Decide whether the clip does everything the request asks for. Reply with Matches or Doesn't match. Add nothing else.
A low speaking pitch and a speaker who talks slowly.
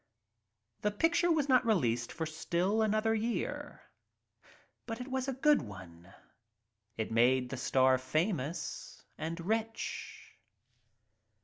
Doesn't match